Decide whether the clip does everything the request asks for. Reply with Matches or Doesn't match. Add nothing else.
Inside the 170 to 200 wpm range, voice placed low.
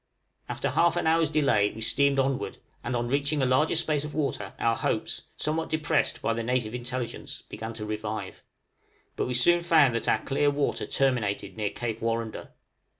Matches